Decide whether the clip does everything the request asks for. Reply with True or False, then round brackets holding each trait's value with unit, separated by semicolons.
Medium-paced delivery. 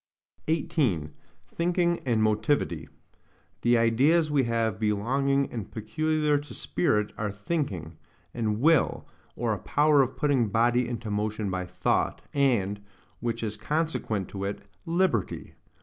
False (130 wpm)